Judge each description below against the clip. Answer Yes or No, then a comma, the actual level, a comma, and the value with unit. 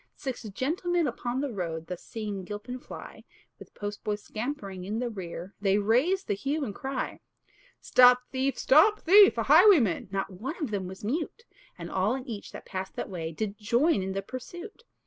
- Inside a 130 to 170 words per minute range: No, average, 185 wpm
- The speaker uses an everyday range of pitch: No, wide, 6.0 semitones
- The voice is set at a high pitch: Yes, high, 230 Hz